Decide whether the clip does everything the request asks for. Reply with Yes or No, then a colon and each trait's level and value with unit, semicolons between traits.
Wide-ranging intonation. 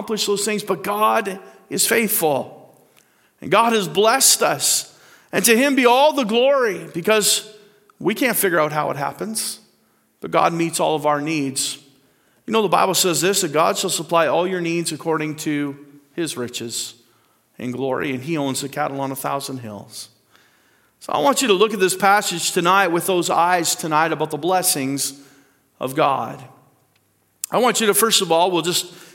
Yes: wide, 6.2 semitones